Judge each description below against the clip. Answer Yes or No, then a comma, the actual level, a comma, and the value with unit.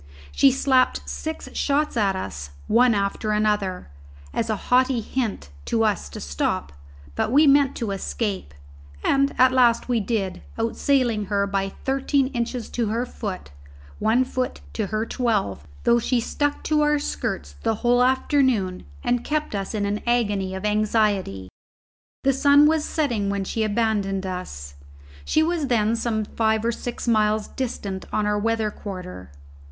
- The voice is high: Yes, high, 225 Hz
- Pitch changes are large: No, average, 4.2 semitones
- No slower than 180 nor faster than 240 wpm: No, average, 160 wpm